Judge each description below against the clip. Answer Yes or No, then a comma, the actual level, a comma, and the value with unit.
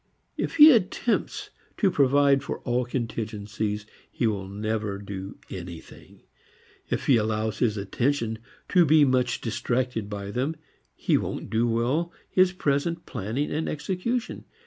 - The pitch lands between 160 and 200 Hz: No, low, 120 Hz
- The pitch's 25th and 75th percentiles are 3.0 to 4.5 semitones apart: No, wide, 5.5 semitones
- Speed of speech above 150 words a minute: No, slow, 135 wpm